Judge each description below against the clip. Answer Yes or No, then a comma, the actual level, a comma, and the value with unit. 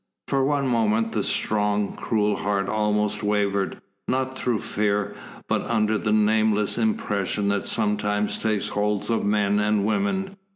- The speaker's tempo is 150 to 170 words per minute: No, average, 140 wpm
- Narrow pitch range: Yes, narrow, 1.5 semitones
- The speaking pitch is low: Yes, low, 105 Hz